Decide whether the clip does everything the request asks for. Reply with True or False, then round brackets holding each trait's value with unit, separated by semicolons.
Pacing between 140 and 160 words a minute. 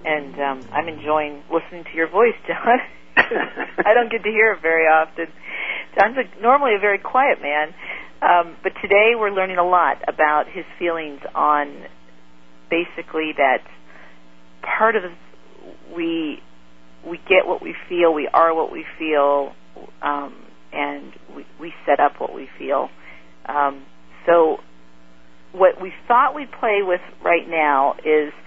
True (150 wpm)